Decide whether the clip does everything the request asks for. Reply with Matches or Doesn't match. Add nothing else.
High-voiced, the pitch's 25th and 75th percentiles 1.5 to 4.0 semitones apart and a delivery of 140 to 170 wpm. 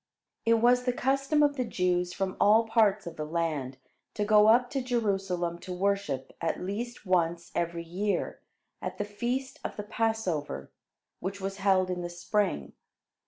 Doesn't match